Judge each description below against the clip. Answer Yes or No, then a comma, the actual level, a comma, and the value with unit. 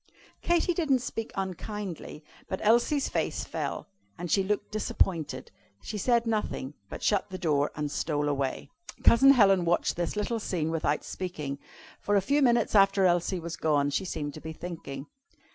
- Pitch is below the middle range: No, medium, 185 Hz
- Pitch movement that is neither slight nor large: No, wide, 5.8 semitones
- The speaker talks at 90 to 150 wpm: No, average, 170 wpm